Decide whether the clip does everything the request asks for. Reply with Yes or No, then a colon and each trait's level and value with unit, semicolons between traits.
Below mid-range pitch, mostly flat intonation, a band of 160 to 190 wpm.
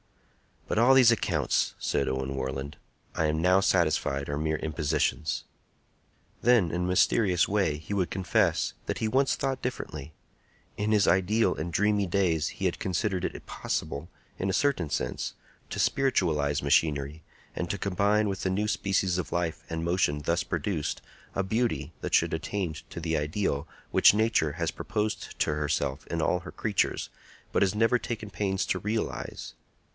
No: very low, 90 Hz; average, 5.2 semitones; average, 165 wpm